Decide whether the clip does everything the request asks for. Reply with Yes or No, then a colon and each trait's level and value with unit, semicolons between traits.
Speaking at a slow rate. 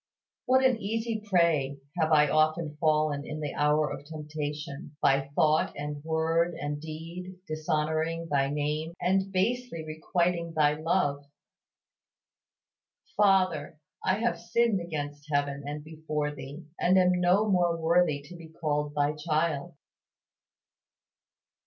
Yes: slow, 125 wpm